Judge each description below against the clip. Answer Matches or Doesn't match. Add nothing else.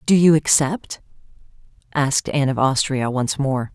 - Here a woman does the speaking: Matches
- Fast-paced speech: Doesn't match